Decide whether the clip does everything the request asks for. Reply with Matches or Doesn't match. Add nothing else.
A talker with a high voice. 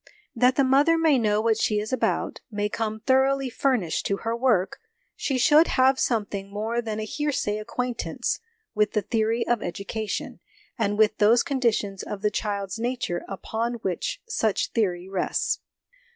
Matches